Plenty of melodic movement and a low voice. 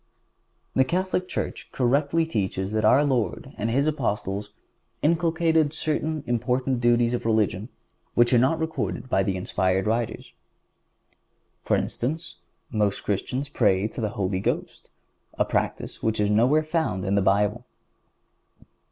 Yes: wide, 6.0 semitones; low, 120 Hz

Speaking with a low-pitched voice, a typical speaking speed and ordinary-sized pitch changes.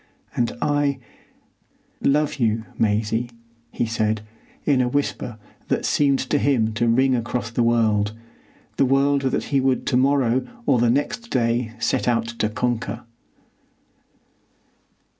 No: low, 120 Hz; slow, 125 wpm; average, 3.0 semitones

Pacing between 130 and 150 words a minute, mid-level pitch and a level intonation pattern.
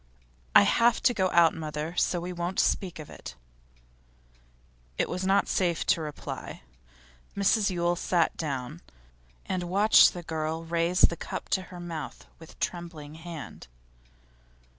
Yes: average, 140 wpm; medium, 170 Hz; narrow, 2.3 semitones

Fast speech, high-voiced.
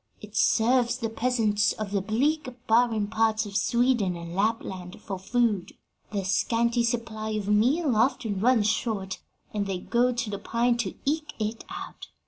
No: average, 160 wpm; high, 225 Hz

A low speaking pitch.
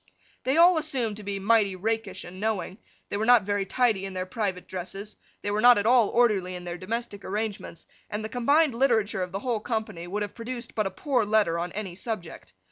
No: high, 210 Hz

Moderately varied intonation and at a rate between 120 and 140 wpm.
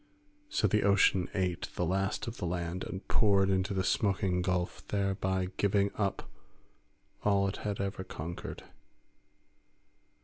No: narrow, 1.5 semitones; slow, 135 wpm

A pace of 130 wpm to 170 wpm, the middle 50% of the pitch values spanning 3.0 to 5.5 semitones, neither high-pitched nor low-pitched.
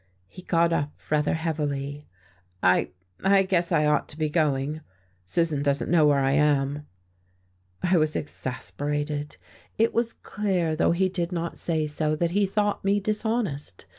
Yes: average, 155 wpm; average, 3.6 semitones; medium, 155 Hz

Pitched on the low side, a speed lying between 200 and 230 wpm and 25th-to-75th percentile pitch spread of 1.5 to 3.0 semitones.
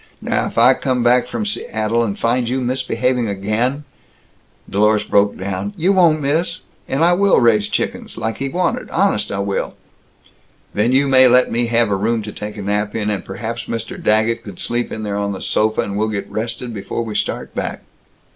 No: low, 115 Hz; fast, 205 wpm; average, 3.4 semitones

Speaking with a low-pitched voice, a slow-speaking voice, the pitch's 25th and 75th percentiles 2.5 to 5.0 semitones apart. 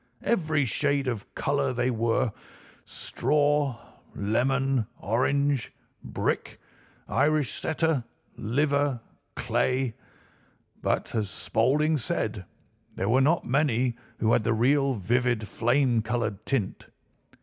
Yes: low, 130 Hz; slow, 100 wpm; average, 3.9 semitones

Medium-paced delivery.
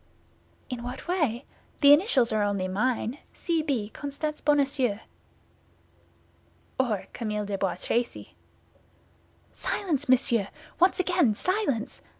No: slow, 105 wpm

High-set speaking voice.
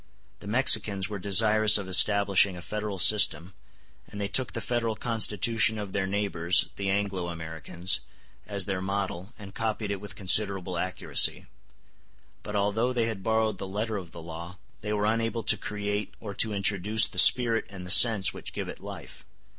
No: low, 100 Hz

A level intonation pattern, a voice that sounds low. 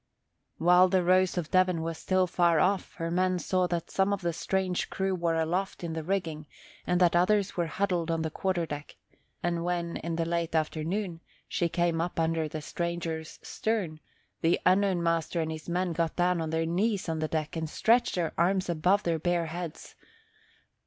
No: narrow, 2.1 semitones; medium, 170 Hz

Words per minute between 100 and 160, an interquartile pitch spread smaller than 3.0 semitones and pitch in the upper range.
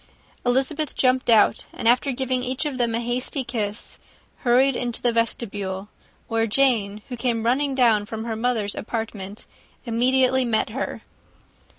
Yes: average, 150 wpm; narrow, 2.5 semitones; high, 240 Hz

